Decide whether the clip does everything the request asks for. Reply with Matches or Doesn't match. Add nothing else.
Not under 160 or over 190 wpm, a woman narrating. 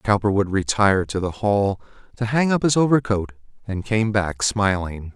Doesn't match